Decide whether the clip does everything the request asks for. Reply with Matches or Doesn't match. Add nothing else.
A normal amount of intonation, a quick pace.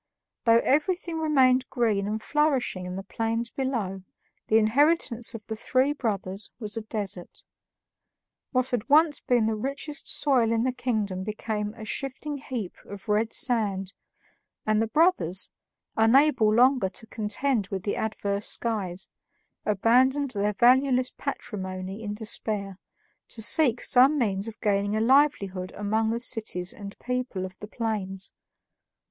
Doesn't match